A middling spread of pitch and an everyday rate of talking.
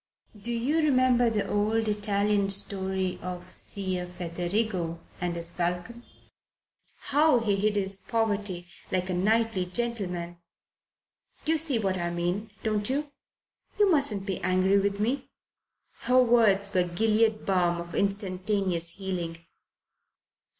No: average, 3.7 semitones; slow, 125 wpm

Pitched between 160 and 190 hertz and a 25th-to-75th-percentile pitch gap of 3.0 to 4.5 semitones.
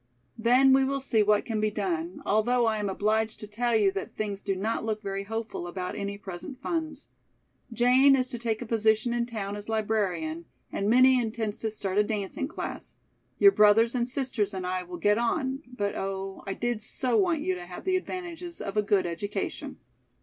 No: high, 215 Hz; average, 3.6 semitones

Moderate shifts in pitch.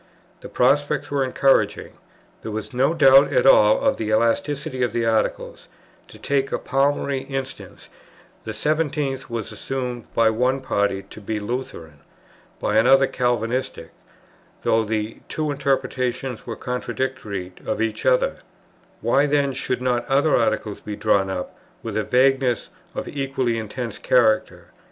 Yes: average, 3.6 semitones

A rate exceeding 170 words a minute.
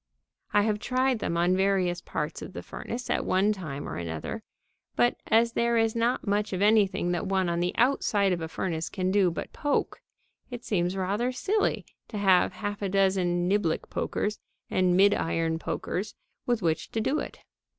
Yes: average, 180 wpm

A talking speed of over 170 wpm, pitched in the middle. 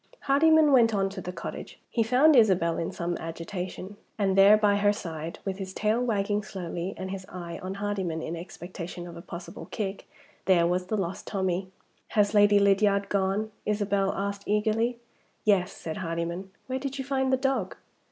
No: average, 180 wpm; high, 195 Hz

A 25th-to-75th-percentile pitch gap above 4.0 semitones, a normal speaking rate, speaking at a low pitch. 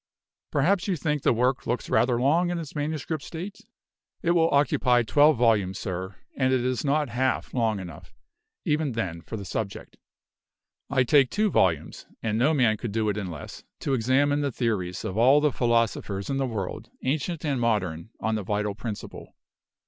Yes: wide, 5.4 semitones; average, 180 wpm; low, 125 Hz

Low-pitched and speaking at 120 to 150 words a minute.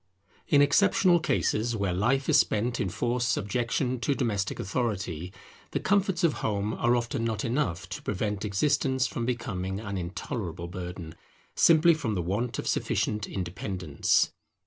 Yes: low, 110 Hz; average, 145 wpm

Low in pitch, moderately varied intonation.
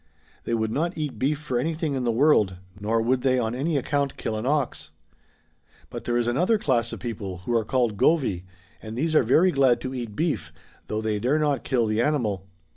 Yes: low, 125 Hz; average, 4.8 semitones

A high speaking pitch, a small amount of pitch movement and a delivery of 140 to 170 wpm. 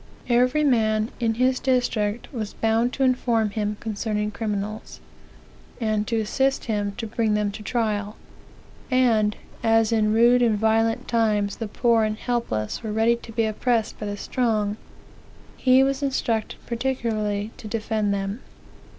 Yes: high, 225 Hz; narrow, 2.3 semitones; average, 150 wpm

